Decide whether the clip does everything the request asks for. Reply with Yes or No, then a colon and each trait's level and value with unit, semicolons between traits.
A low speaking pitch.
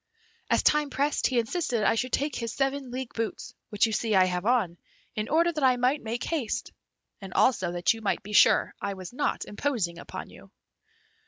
No: high, 235 Hz